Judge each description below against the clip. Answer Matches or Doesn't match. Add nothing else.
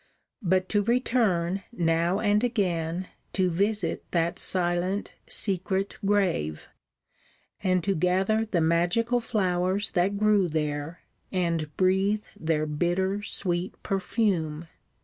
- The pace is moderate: Doesn't match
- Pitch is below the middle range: Doesn't match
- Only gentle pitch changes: Doesn't match